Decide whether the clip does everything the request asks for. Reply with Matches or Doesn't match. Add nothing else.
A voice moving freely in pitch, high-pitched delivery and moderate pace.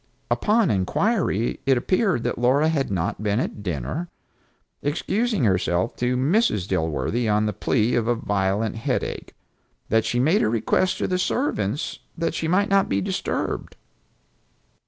Doesn't match